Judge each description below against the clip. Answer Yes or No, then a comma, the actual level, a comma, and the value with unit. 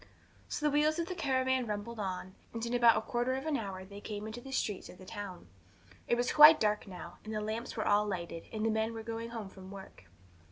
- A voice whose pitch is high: Yes, high, 220 Hz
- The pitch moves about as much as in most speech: Yes, average, 3.3 semitones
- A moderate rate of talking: No, fast, 245 wpm